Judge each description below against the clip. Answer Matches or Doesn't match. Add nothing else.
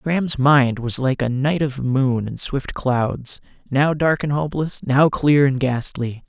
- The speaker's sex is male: Matches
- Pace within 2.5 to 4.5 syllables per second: Matches